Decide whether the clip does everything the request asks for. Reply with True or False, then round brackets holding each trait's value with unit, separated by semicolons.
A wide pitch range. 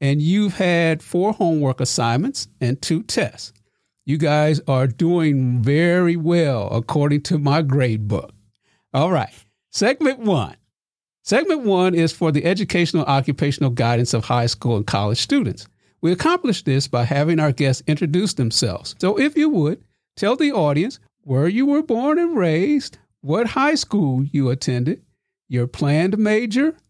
True (6.5 semitones)